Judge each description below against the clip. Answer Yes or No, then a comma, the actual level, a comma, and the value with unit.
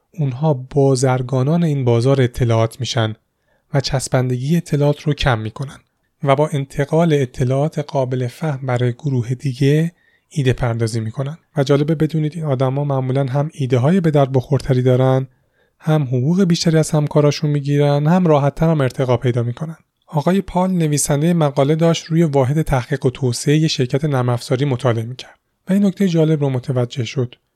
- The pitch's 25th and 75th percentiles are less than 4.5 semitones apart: Yes, average, 3.2 semitones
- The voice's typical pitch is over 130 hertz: Yes, medium, 140 Hz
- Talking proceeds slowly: No, average, 150 wpm